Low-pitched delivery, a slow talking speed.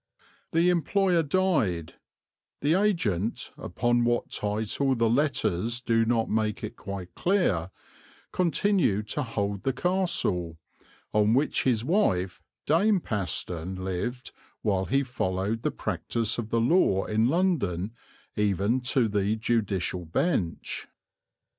Yes: low, 115 Hz; slow, 120 wpm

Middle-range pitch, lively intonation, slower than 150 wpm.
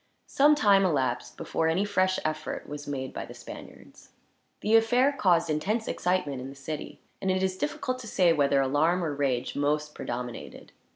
No: medium, 165 Hz; wide, 5.7 semitones; average, 175 wpm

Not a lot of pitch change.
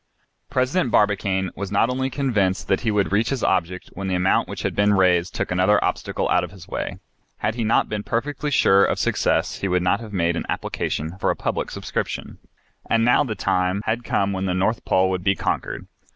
No: average, 3.5 semitones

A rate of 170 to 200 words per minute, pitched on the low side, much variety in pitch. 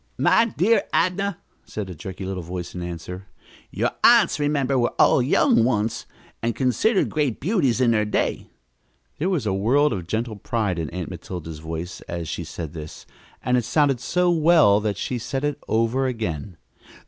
Yes: average, 175 wpm; low, 115 Hz; wide, 7.9 semitones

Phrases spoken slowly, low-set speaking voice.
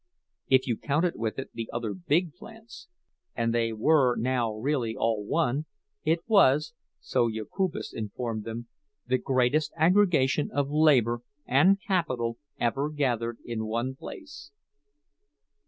Yes: slow, 120 wpm; low, 130 Hz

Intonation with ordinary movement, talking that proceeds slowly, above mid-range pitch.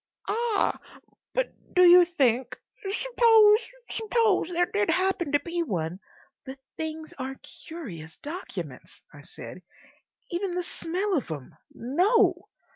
No: wide, 7.4 semitones; slow, 120 wpm; very high, 350 Hz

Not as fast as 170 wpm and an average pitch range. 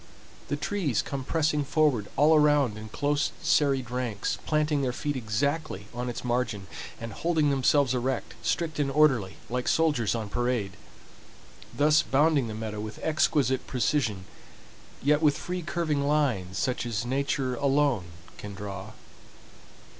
Yes: average, 140 wpm; average, 4.5 semitones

